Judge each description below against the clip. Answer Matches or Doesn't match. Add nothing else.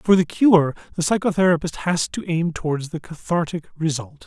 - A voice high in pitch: Doesn't match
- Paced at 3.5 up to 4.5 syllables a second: Doesn't match